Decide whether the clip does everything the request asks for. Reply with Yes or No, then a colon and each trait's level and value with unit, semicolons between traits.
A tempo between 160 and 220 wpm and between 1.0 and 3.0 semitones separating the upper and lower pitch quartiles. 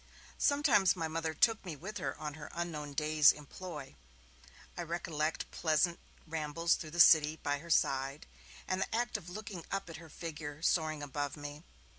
Yes: average, 170 wpm; narrow, 2.6 semitones